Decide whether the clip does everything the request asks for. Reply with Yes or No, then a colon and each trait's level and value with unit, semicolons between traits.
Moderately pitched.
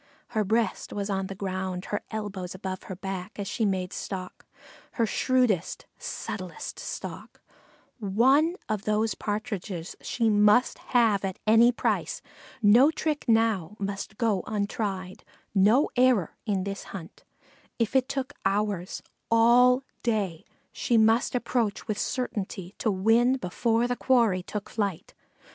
No: high, 210 Hz